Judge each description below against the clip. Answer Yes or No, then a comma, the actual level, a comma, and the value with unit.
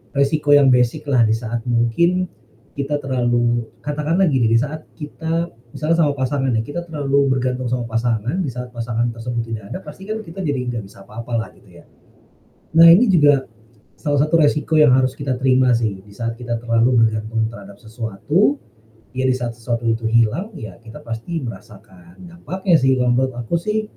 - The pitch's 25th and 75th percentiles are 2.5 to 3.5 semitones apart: No, average, 4.5 semitones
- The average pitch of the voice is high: No, low, 125 Hz